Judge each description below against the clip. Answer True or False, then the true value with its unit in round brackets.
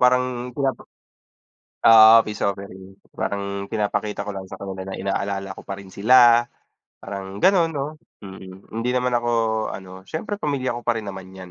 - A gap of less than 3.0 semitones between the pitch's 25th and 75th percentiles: False (4.2 semitones)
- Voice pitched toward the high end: False (100 Hz)